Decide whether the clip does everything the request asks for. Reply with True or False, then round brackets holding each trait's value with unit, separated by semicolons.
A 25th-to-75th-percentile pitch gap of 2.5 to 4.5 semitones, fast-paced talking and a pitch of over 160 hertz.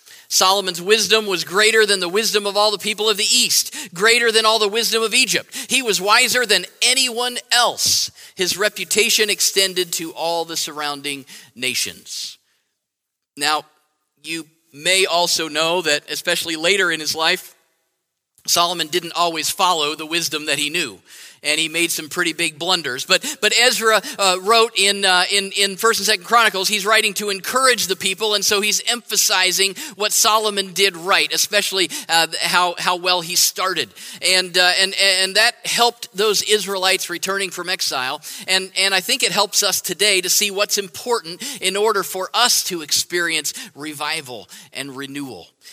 False (3.9 semitones; 170 wpm; 190 Hz)